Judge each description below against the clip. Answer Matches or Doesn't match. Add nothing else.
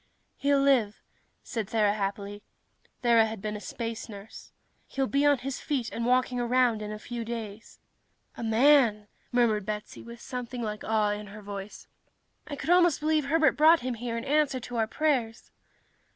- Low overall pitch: Doesn't match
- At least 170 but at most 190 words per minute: Matches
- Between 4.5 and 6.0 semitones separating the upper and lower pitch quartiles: Doesn't match